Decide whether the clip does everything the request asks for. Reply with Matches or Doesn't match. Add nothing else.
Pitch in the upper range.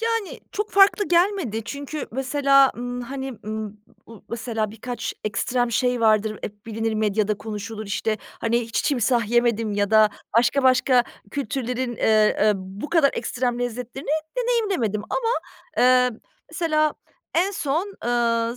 Matches